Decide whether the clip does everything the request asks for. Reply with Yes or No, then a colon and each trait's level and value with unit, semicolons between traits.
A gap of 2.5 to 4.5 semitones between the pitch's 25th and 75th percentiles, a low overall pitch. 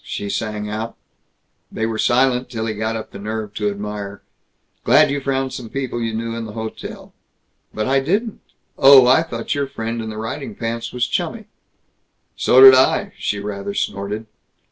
Yes: average, 3.5 semitones; low, 115 Hz